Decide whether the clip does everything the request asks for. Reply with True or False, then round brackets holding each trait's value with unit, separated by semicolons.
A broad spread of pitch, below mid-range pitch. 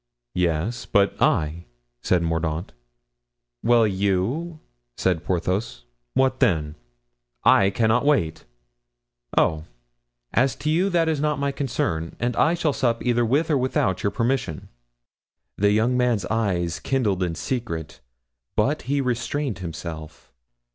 True (7.3 semitones; 110 Hz)